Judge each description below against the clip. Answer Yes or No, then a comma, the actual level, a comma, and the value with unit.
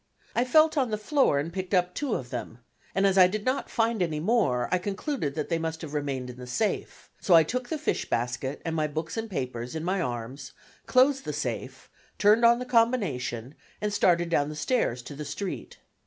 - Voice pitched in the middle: Yes, medium, 175 Hz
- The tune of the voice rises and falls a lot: Yes, wide, 8.1 semitones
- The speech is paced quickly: Yes, fast, 215 wpm